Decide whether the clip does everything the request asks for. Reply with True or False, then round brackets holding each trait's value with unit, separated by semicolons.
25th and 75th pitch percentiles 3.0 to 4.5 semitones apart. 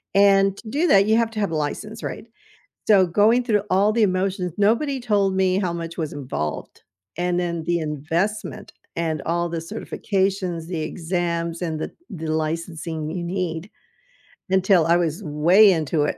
True (3.5 semitones)